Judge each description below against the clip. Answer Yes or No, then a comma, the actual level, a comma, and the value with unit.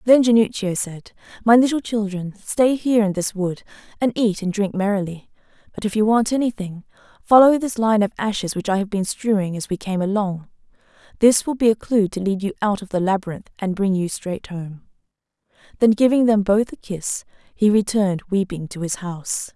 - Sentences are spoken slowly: No, average, 195 wpm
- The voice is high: Yes, high, 205 Hz